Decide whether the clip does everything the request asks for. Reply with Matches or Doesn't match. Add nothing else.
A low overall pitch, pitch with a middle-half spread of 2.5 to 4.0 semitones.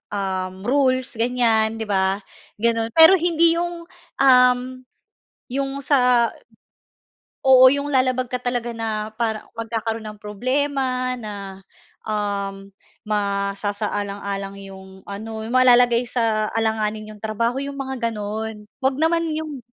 Doesn't match